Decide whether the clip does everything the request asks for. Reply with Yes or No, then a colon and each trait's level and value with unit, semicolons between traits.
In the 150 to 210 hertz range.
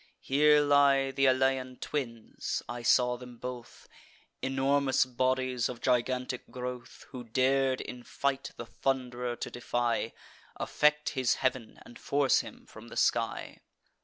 No: low, 130 Hz